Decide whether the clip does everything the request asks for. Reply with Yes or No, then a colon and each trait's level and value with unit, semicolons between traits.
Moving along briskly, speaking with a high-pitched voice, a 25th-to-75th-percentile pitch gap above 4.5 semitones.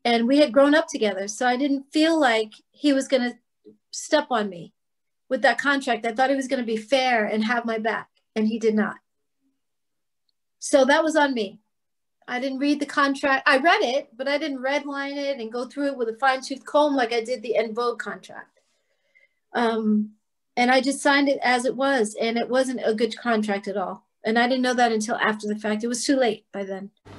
No: fast, 225 wpm; very high, 250 Hz; average, 3.8 semitones